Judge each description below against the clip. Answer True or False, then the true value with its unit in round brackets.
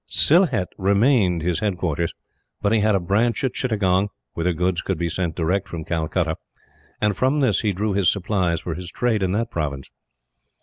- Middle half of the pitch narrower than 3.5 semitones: False (3.8 semitones)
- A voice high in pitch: False (95 Hz)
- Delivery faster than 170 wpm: True (180 wpm)